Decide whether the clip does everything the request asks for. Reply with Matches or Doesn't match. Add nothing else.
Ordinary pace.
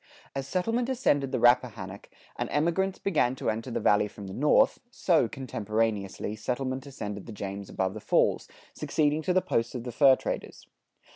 Matches